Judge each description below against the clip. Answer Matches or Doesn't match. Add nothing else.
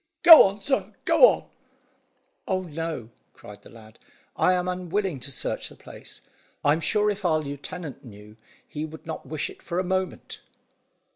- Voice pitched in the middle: Matches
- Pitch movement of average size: Matches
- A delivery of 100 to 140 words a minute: Doesn't match